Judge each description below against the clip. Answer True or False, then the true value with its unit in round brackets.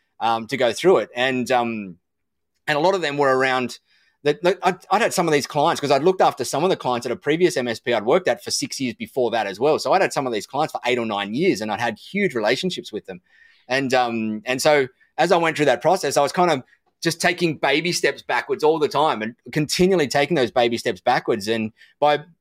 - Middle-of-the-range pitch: True (145 Hz)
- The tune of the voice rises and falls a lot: True (6.2 semitones)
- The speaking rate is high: True (255 wpm)